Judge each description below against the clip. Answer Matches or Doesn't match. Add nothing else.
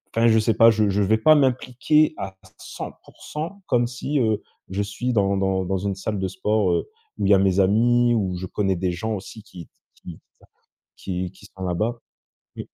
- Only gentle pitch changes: Doesn't match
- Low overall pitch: Matches